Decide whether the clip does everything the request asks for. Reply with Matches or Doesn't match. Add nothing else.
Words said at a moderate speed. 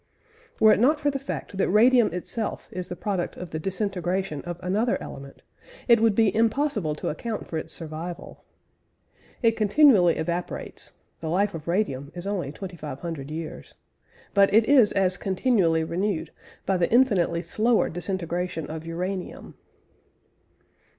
Matches